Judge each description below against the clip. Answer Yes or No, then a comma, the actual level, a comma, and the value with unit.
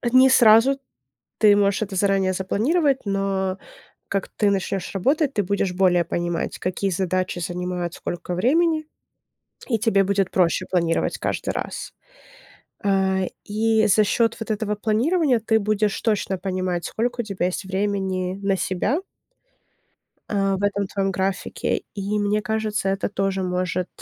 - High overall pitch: Yes, high, 195 Hz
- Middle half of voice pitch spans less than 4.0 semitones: Yes, narrow, 2.6 semitones